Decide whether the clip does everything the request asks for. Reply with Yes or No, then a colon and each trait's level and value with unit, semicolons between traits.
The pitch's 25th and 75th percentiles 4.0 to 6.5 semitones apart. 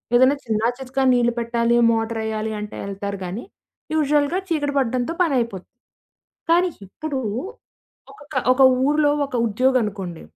Yes: average, 4.6 semitones